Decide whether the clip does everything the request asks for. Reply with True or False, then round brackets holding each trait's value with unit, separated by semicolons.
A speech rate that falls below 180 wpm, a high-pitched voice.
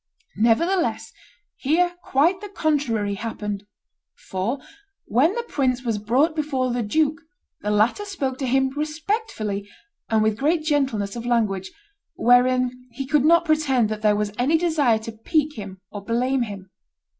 True (150 wpm; 255 Hz)